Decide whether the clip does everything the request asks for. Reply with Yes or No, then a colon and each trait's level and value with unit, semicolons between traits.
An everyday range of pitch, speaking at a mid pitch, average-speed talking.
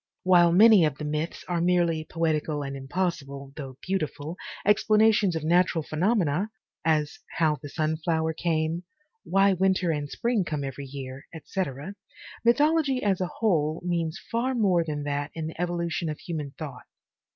Yes: average, 3.7 semitones; medium, 165 Hz; average, 155 wpm